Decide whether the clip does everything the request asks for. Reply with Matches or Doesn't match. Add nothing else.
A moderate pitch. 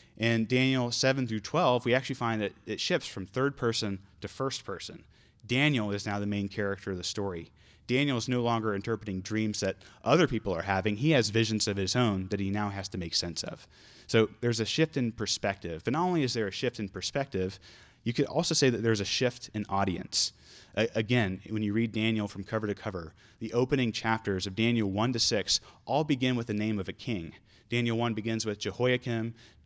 Doesn't match